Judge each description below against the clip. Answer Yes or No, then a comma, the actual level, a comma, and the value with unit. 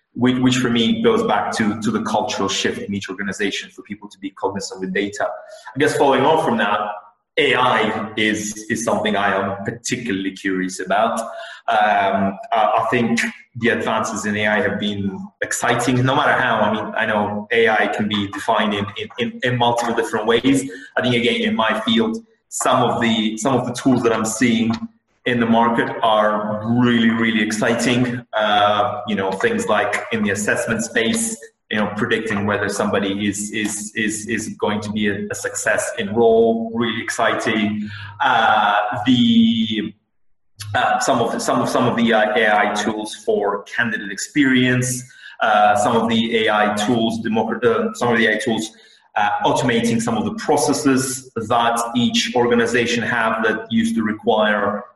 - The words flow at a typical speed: Yes, average, 170 wpm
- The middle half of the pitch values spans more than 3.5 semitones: No, average, 3.0 semitones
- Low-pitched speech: Yes, low, 115 Hz